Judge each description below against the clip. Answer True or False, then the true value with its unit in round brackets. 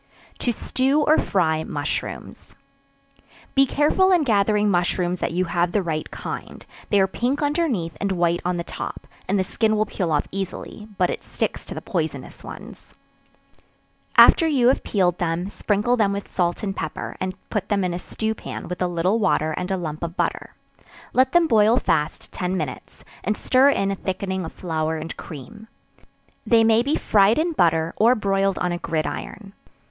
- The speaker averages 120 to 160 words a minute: False (185 wpm)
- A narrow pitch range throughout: False (4.3 semitones)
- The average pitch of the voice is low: False (195 Hz)